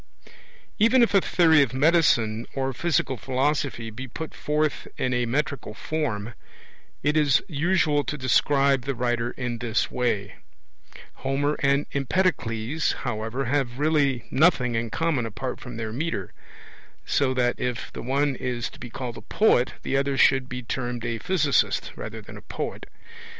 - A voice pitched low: Yes, low, 130 Hz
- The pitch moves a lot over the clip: No, average, 3.5 semitones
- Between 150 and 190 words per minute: Yes, average, 155 wpm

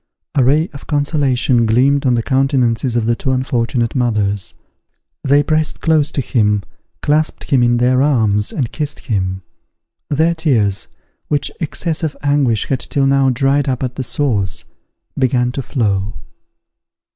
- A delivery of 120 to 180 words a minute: Yes, average, 150 wpm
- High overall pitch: No, low, 130 Hz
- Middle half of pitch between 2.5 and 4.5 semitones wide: Yes, average, 3.6 semitones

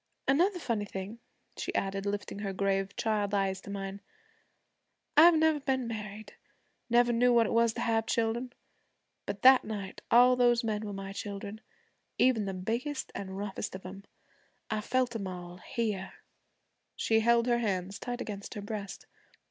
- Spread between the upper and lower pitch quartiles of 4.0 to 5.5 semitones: No, average, 3.3 semitones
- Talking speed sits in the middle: Yes, average, 165 wpm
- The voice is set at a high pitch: Yes, high, 215 Hz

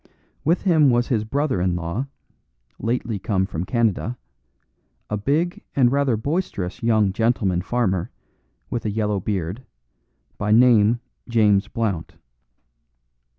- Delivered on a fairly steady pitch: No, average, 4.1 semitones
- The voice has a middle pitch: No, low, 110 Hz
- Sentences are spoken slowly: Yes, slow, 120 wpm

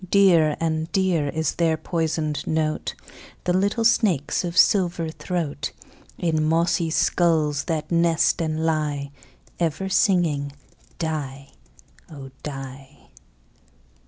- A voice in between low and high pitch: Yes, medium, 160 Hz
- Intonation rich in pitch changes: No, narrow, 2.4 semitones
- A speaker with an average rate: No, slow, 105 wpm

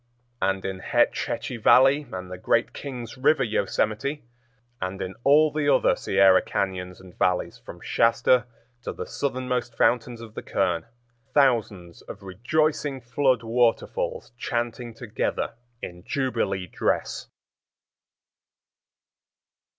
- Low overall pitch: Yes, low, 115 Hz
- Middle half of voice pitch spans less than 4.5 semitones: No, wide, 5.4 semitones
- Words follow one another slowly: Yes, slow, 120 wpm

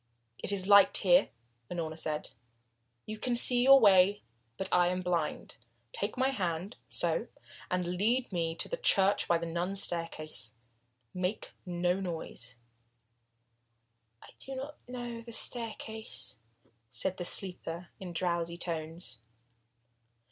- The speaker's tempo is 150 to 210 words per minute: No, slow, 135 wpm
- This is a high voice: No, medium, 180 Hz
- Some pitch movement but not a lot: Yes, average, 4.3 semitones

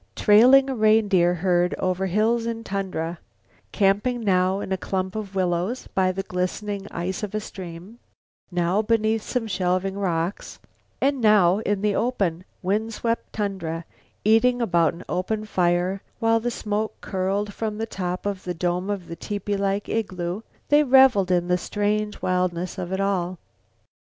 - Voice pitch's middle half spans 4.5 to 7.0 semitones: No, average, 3.1 semitones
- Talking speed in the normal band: Yes, average, 160 wpm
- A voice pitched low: No, high, 195 Hz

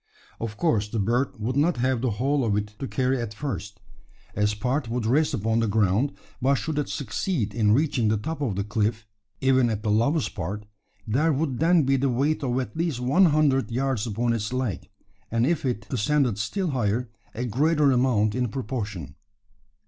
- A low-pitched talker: Yes, low, 125 Hz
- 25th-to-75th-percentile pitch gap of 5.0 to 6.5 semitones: No, average, 4.4 semitones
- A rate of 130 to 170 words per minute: No, average, 195 wpm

